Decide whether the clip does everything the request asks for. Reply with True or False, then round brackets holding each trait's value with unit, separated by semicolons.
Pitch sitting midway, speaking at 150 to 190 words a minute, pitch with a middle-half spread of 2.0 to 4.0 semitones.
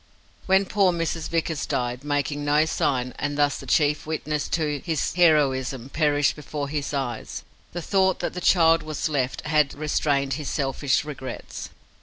True (150 Hz; 160 wpm; 2.4 semitones)